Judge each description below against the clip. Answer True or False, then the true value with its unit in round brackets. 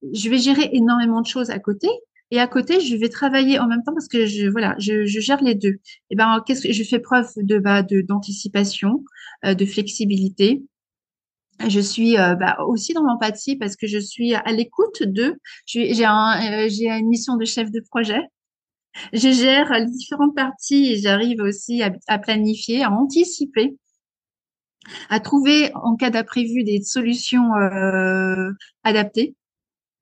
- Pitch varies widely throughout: False (3.8 semitones)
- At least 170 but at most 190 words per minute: True (175 wpm)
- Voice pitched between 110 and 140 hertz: False (230 Hz)